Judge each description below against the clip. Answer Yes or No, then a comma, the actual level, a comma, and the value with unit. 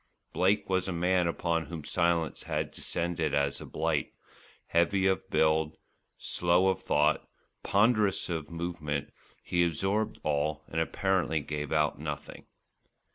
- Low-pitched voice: Yes, very low, 85 Hz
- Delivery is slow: Yes, slow, 130 wpm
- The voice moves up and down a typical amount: Yes, average, 3.2 semitones